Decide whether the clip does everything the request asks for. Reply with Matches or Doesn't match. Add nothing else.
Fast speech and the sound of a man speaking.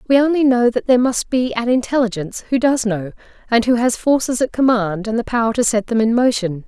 Doesn't match